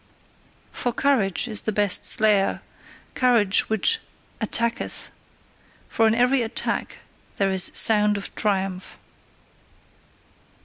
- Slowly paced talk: Yes, slow, 100 wpm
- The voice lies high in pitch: Yes, high, 215 Hz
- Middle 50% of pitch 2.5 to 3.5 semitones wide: Yes, average, 2.9 semitones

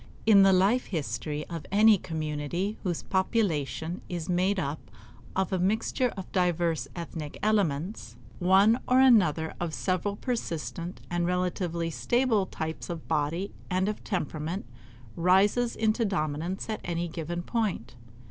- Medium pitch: Yes, medium, 180 Hz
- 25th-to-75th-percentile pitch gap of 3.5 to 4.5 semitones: Yes, average, 3.9 semitones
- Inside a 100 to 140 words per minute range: Yes, slow, 135 wpm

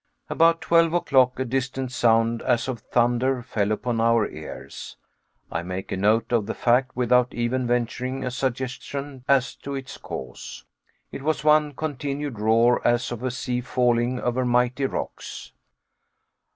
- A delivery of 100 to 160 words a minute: Yes, average, 150 wpm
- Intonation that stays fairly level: Yes, narrow, 2.1 semitones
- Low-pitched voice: Yes, low, 125 Hz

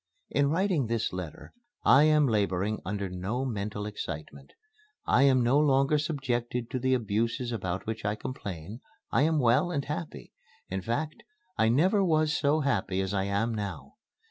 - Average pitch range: No, wide, 5.9 semitones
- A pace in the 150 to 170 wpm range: Yes, average, 165 wpm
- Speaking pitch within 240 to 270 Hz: No, low, 120 Hz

